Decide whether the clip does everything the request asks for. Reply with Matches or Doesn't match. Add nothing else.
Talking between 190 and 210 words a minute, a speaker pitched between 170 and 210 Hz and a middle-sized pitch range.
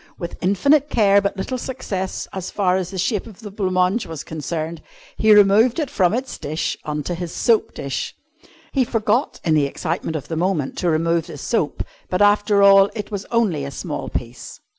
Matches